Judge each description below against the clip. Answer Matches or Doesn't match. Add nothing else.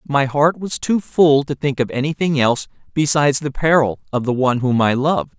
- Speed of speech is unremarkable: Doesn't match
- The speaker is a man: Matches